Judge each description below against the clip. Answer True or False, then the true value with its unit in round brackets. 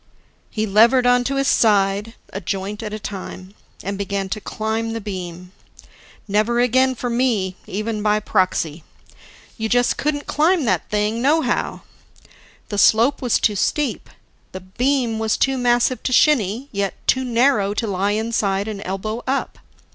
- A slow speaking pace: False (155 wpm)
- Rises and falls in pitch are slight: False (3.8 semitones)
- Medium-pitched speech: False (220 Hz)